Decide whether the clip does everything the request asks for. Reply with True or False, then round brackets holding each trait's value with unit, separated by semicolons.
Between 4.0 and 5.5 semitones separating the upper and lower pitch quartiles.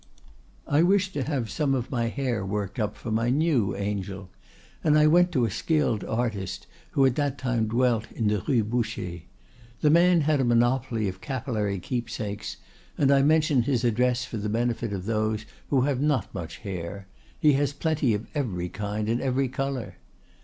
True (4.6 semitones)